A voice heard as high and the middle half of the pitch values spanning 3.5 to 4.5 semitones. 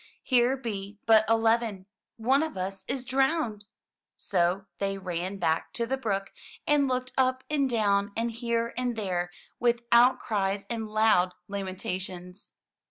Yes: high, 220 Hz; average, 4.0 semitones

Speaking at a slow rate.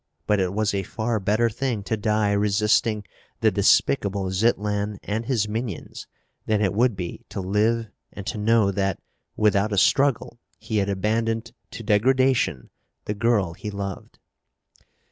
No: average, 150 wpm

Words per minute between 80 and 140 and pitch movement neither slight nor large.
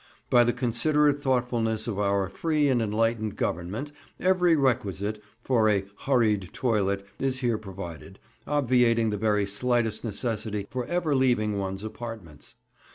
Yes: slow, 135 wpm; average, 4.0 semitones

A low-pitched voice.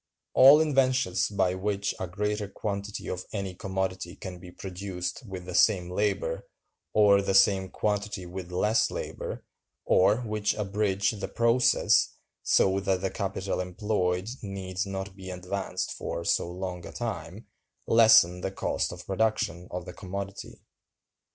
Yes: very low, 95 Hz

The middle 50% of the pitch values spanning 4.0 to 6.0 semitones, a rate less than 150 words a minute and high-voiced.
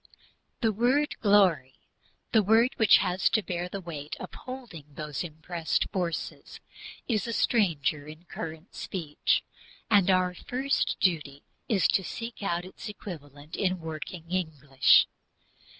No: average, 4.9 semitones; slow, 135 wpm; medium, 180 Hz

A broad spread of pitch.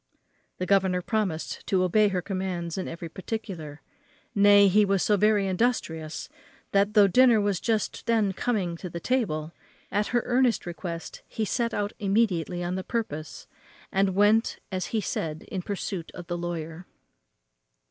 No: average, 3.5 semitones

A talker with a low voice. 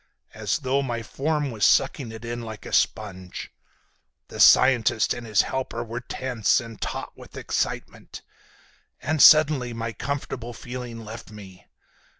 Yes: low, 120 Hz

